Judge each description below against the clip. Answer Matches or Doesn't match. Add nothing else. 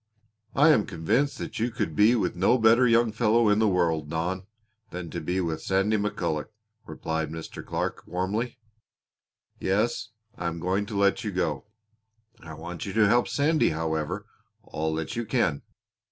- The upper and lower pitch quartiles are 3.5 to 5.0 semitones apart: Doesn't match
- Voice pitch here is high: Doesn't match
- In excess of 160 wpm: Matches